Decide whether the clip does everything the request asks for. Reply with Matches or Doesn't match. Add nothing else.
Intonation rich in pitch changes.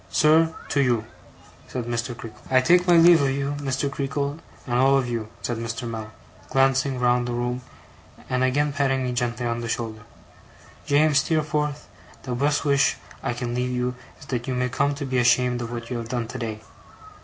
Doesn't match